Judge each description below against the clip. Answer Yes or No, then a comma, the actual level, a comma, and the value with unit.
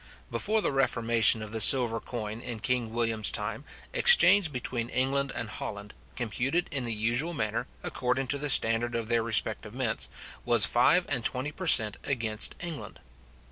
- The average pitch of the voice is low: Yes, low, 120 Hz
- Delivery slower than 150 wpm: No, average, 165 wpm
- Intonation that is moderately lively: Yes, average, 3.3 semitones